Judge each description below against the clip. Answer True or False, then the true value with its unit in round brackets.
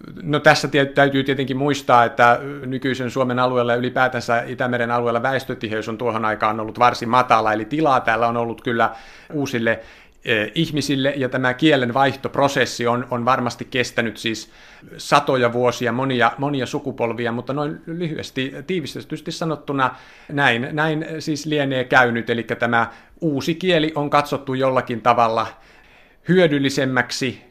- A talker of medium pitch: False (130 Hz)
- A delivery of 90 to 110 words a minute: False (135 wpm)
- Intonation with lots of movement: False (3.2 semitones)